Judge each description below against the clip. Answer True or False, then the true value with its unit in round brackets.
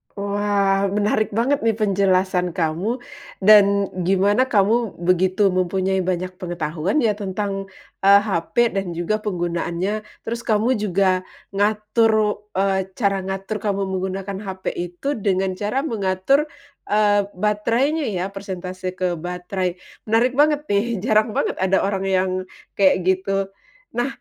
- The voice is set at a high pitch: True (195 Hz)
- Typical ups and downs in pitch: False (2.3 semitones)